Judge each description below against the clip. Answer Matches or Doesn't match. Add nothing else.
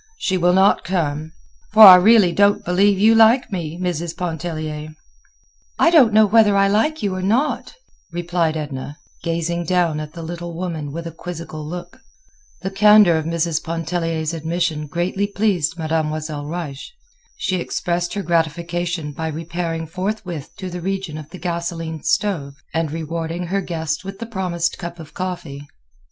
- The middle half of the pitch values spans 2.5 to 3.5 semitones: Matches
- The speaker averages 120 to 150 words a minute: Doesn't match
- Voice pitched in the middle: Matches